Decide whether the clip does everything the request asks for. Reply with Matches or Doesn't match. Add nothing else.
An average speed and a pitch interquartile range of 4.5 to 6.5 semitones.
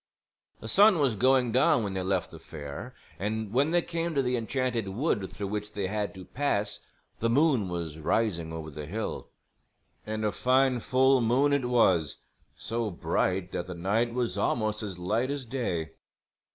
Matches